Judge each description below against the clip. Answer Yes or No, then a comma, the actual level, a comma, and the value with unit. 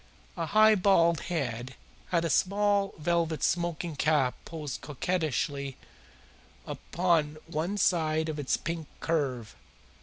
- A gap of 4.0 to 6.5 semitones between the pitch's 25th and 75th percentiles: No, average, 2.9 semitones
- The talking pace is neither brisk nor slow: No, slow, 115 wpm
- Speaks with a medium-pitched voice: Yes, medium, 165 Hz